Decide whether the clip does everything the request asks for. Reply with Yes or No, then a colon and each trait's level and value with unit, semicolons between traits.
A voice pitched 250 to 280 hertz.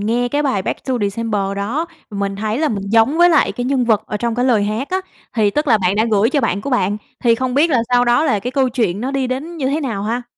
No: high, 240 Hz